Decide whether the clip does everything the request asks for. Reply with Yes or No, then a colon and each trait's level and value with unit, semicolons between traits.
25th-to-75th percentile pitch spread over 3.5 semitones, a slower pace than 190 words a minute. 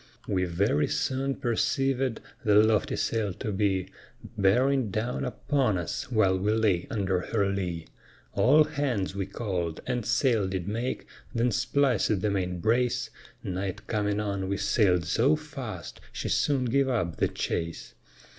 Yes: average, 4.9 semitones; average, 145 wpm